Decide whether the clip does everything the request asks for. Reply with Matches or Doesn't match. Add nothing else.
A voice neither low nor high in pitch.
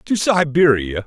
Matches